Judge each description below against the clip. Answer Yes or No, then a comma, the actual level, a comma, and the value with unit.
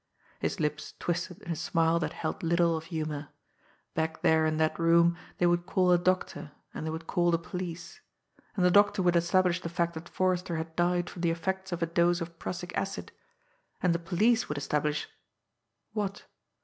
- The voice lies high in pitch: No, medium, 170 Hz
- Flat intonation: Yes, narrow, 1.8 semitones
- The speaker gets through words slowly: No, average, 190 wpm